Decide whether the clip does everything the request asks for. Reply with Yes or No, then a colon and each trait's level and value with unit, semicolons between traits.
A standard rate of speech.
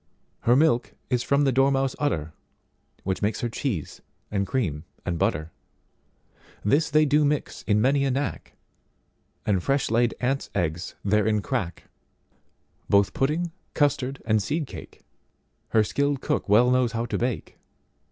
No: slow, 130 wpm